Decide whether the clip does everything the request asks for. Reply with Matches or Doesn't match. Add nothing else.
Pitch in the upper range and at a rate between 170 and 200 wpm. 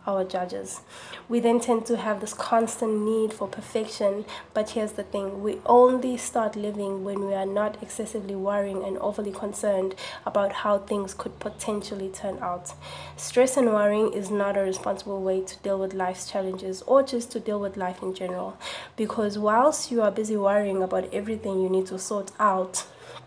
Matches